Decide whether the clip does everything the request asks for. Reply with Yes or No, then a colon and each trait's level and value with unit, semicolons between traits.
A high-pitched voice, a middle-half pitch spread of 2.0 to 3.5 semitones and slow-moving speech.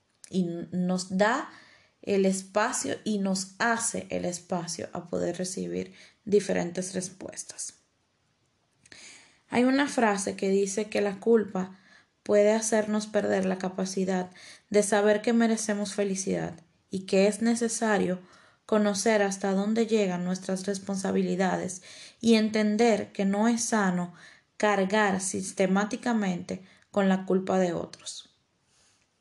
Yes: high, 200 Hz; narrow, 2.4 semitones; slow, 115 wpm